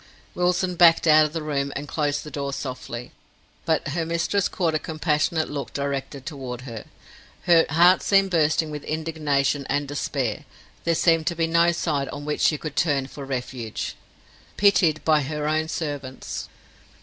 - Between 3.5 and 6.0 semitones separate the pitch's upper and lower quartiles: No, average, 2.8 semitones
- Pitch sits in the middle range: Yes, medium, 150 Hz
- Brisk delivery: No, average, 165 wpm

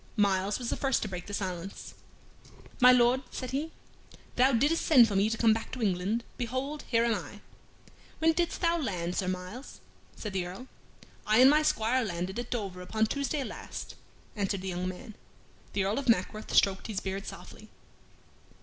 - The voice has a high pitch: Yes, high, 220 Hz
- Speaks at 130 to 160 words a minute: No, average, 185 wpm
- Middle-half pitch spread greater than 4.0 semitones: Yes, average, 5.1 semitones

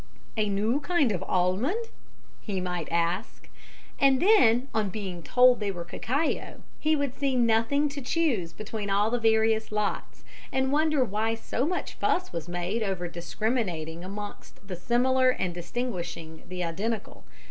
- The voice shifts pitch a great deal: Yes, wide, 6.1 semitones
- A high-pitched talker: Yes, high, 220 Hz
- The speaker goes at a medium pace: Yes, average, 150 wpm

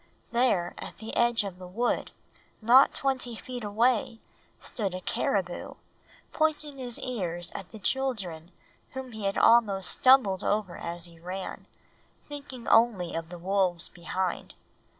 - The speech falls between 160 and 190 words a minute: No, average, 140 wpm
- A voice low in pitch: No, high, 210 Hz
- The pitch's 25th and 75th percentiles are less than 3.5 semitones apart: No, wide, 5.4 semitones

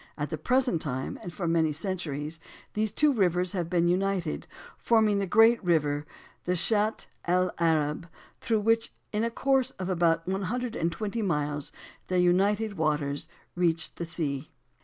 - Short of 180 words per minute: Yes, average, 160 wpm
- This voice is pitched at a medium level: Yes, medium, 180 Hz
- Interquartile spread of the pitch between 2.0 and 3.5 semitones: No, average, 4.6 semitones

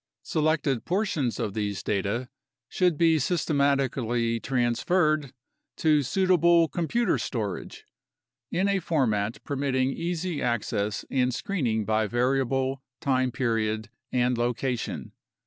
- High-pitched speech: No, low, 130 Hz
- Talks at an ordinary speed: No, slow, 105 wpm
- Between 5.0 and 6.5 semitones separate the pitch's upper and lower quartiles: Yes, wide, 5.4 semitones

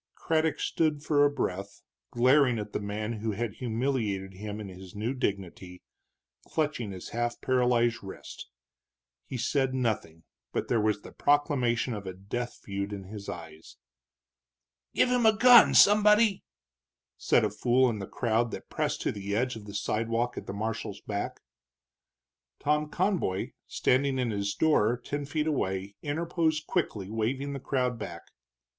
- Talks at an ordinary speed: Yes, average, 155 wpm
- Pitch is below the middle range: Yes, low, 120 Hz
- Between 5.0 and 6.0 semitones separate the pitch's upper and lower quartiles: Yes, wide, 5.6 semitones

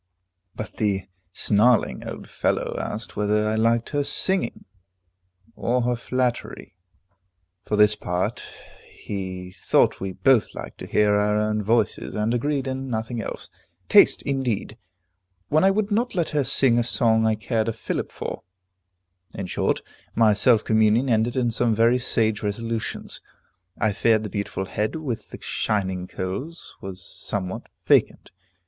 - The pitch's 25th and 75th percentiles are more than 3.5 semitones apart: No, average, 2.9 semitones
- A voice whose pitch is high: No, low, 110 Hz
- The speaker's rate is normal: Yes, average, 150 wpm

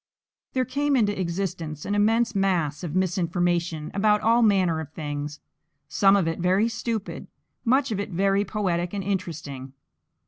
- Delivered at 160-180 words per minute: No, average, 150 wpm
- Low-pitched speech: No, high, 190 Hz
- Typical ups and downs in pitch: Yes, average, 4.0 semitones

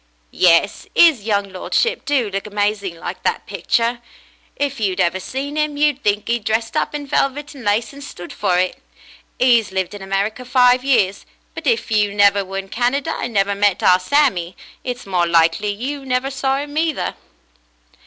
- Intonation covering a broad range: Yes, wide, 5.7 semitones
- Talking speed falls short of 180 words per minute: No, average, 185 wpm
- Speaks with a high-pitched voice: Yes, high, 225 Hz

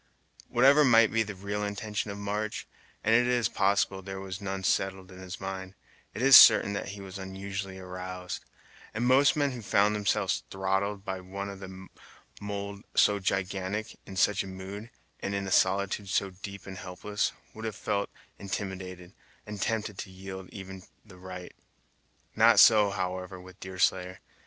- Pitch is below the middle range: Yes, low, 100 Hz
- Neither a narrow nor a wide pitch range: No, narrow, 1.7 semitones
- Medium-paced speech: Yes, average, 170 wpm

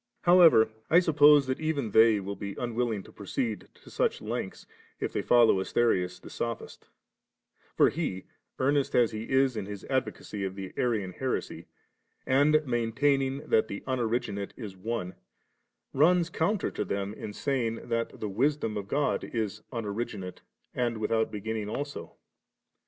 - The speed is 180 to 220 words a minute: No, average, 150 wpm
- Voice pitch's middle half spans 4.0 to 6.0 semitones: Yes, average, 4.7 semitones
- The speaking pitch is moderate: No, low, 115 Hz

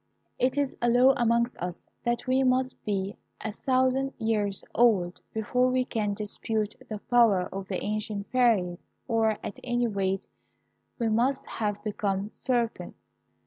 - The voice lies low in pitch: No, high, 225 Hz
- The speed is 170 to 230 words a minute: No, average, 145 wpm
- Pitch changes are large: No, average, 3.4 semitones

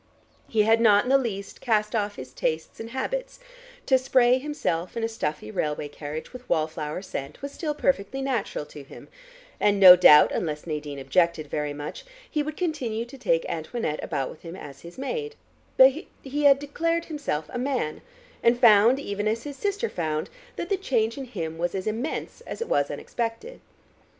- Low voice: No, high, 225 Hz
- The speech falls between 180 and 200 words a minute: Yes, average, 190 wpm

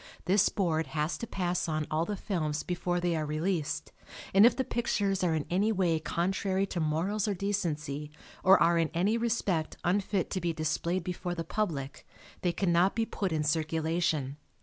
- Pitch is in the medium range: Yes, medium, 175 Hz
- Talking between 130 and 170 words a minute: No, average, 180 wpm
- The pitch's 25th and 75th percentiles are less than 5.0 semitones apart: Yes, average, 3.7 semitones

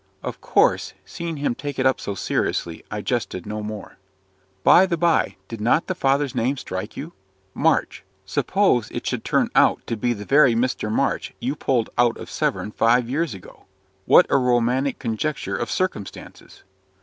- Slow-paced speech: No, average, 175 wpm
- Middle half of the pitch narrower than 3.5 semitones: No, average, 4.6 semitones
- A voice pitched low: Yes, low, 125 Hz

